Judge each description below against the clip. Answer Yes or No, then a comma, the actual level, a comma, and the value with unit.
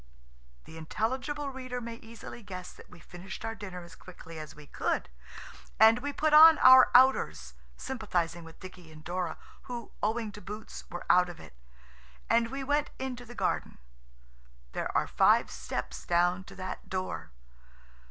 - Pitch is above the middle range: Yes, high, 210 Hz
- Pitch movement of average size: No, wide, 6.1 semitones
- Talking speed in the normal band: Yes, average, 160 wpm